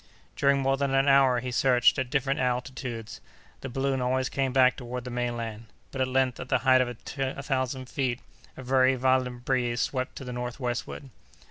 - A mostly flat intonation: Yes, narrow, 1.5 semitones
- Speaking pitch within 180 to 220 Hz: No, low, 130 Hz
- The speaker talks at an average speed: Yes, average, 190 wpm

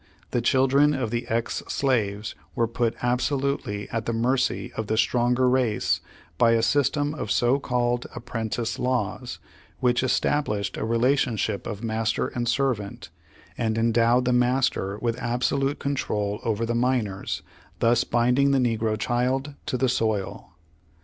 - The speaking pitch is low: Yes, low, 120 Hz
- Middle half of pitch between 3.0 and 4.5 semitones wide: No, narrow, 2.5 semitones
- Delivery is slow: No, average, 150 wpm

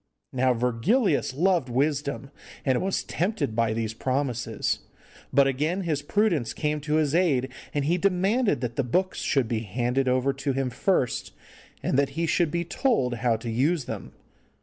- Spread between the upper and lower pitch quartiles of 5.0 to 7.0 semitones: Yes, wide, 5.5 semitones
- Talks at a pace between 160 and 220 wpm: Yes, average, 170 wpm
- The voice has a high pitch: No, medium, 140 Hz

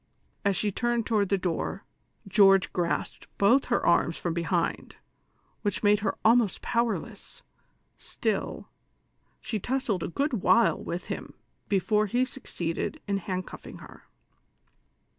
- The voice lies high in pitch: Yes, high, 205 Hz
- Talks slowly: Yes, slow, 130 wpm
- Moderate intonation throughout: Yes, average, 4.2 semitones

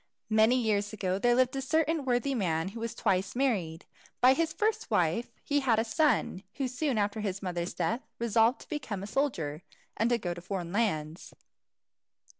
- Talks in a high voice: Yes, high, 225 Hz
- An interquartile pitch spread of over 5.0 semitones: Yes, wide, 5.5 semitones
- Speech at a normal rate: Yes, average, 180 wpm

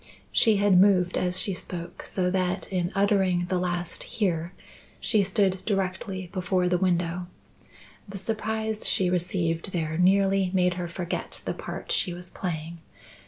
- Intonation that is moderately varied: No, narrow, 1.7 semitones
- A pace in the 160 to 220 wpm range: No, average, 150 wpm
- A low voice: No, medium, 180 Hz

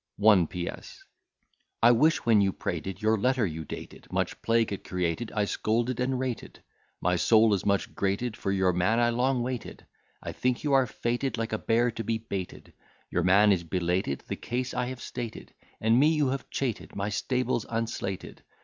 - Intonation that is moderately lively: Yes, average, 4.1 semitones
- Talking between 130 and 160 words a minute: No, average, 185 wpm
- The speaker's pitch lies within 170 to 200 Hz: No, low, 110 Hz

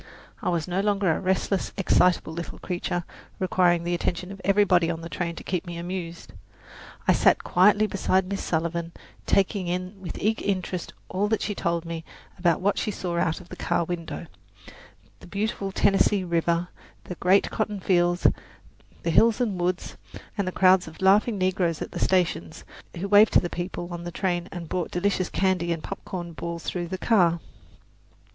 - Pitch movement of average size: No, narrow, 2.2 semitones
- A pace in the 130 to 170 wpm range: No, average, 180 wpm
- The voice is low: No, medium, 180 Hz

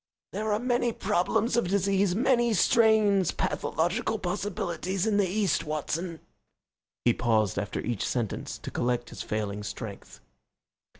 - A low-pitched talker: No, medium, 185 Hz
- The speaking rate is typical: No, slow, 130 wpm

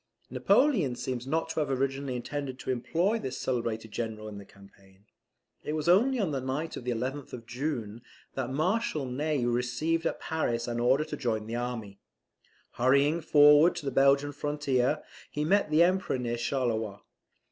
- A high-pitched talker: No, low, 135 Hz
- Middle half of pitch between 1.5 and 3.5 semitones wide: No, average, 4.2 semitones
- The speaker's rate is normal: Yes, average, 170 wpm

